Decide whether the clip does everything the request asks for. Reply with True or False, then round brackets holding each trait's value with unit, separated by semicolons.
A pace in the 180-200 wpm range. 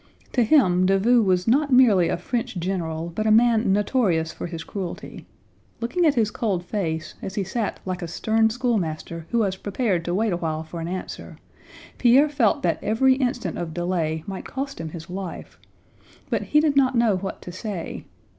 True (185 wpm)